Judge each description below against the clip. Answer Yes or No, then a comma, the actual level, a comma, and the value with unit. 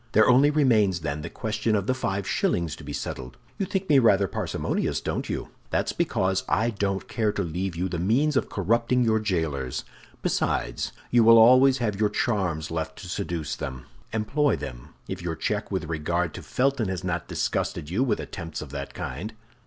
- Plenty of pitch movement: Yes, wide, 5.7 semitones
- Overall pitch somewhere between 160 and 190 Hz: No, low, 100 Hz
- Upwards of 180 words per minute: Yes, average, 195 wpm